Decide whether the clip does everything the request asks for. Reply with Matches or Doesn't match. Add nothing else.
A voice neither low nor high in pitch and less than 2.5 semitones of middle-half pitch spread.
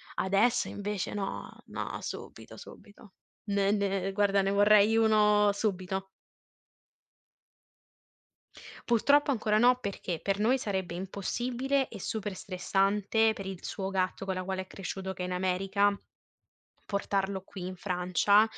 Doesn't match